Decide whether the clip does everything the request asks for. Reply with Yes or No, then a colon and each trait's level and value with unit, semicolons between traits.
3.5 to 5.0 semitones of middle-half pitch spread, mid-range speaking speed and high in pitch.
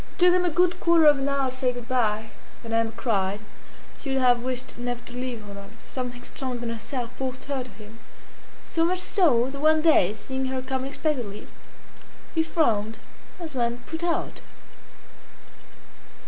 Yes: average, 3.9 semitones; average, 175 wpm; very high, 255 Hz